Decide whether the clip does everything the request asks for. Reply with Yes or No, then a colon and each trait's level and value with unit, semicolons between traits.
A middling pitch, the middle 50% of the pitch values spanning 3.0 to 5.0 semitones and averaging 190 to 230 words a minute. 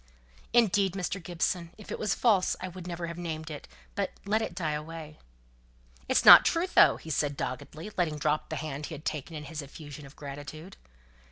Yes: medium, 160 Hz; average, 3.4 semitones; average, 195 wpm